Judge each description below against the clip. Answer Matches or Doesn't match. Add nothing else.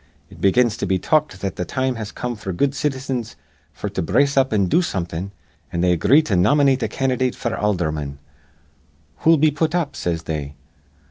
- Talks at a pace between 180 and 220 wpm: Matches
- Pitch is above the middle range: Doesn't match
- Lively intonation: Matches